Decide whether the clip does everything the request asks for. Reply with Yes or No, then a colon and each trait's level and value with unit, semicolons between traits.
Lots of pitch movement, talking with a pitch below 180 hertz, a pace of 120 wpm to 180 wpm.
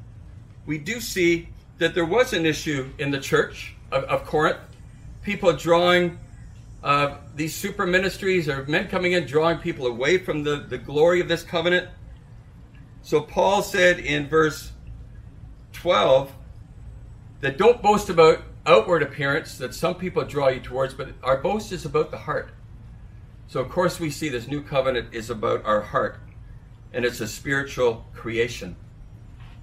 Yes: wide, 6.2 semitones; medium, 140 Hz; average, 155 wpm